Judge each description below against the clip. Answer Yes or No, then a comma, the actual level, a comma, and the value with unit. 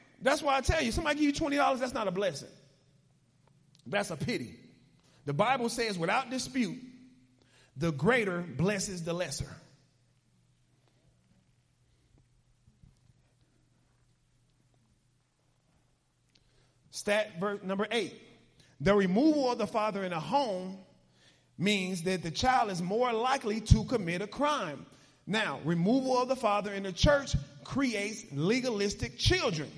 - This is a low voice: No, medium, 185 Hz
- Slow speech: Yes, slow, 120 wpm